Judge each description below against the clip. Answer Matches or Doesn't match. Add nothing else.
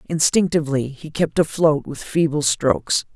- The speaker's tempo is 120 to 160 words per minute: Matches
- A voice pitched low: Doesn't match